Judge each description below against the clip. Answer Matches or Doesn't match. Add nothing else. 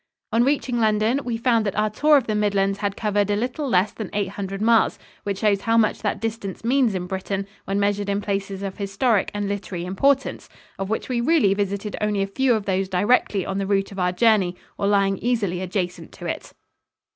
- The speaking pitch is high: Matches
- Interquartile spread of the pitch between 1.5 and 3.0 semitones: Matches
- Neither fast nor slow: Doesn't match